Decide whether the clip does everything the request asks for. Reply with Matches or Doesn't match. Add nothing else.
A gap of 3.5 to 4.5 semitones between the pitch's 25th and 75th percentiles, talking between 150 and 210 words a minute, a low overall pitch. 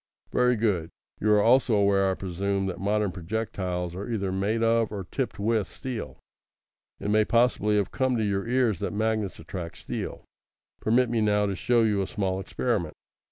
Doesn't match